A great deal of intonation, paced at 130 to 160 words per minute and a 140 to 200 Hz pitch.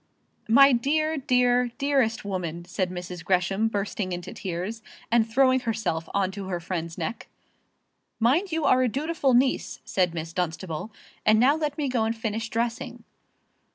No: wide, 5.8 semitones; average, 155 wpm; high, 225 Hz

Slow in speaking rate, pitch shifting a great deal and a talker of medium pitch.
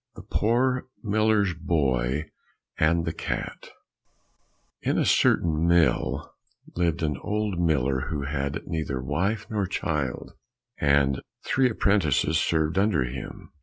No: slow, 125 wpm; wide, 6.0 semitones; very low, 80 Hz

